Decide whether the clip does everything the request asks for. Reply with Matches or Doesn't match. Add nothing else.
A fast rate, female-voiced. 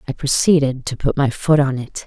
Matches